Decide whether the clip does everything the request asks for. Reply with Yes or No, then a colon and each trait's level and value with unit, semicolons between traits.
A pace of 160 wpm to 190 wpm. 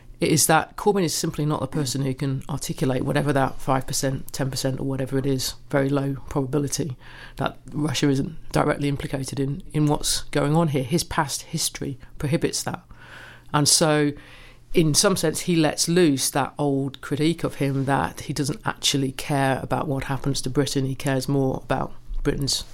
Yes: average, 175 wpm